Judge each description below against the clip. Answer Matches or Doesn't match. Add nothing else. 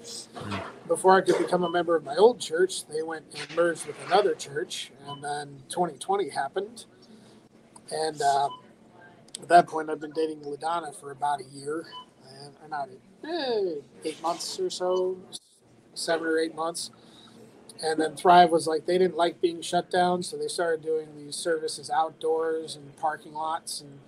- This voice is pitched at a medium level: Matches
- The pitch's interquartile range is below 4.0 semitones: Matches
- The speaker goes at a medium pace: Matches